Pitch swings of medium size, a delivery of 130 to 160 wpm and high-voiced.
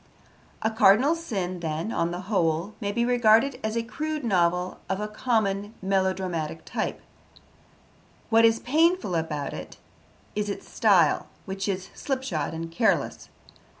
Yes: average, 4.5 semitones; average, 140 wpm; high, 200 Hz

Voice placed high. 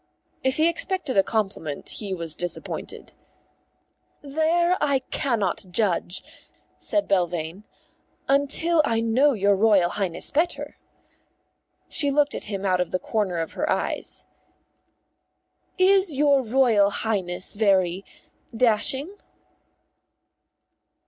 Yes: high, 220 Hz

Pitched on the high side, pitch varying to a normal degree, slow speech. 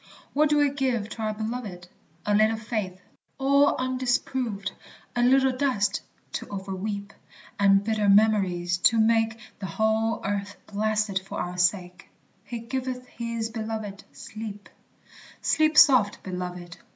Yes: high, 215 Hz; average, 3.6 semitones; slow, 130 wpm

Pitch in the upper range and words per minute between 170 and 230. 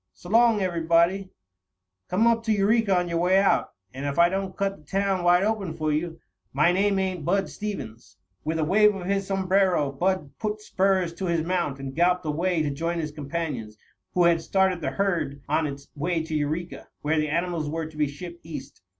No: medium, 175 Hz; average, 200 wpm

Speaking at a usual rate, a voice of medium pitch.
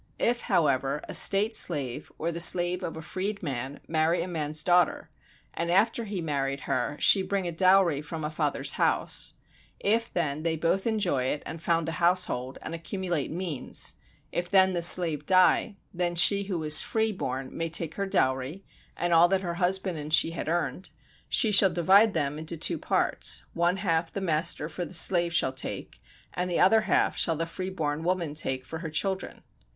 Yes: average, 190 wpm; medium, 170 Hz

